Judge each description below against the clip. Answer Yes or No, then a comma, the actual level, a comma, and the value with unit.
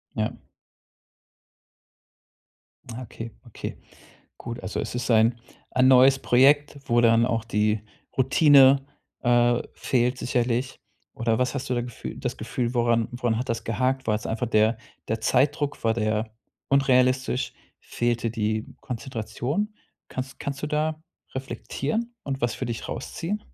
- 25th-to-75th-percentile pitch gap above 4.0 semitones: No, narrow, 2.6 semitones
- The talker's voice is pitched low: Yes, low, 125 Hz